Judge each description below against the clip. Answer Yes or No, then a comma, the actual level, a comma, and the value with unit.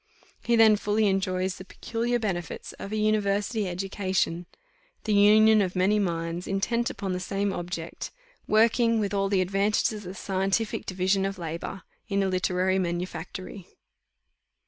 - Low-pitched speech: No, high, 195 Hz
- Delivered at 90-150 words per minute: Yes, average, 145 wpm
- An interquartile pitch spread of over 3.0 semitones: No, narrow, 2.5 semitones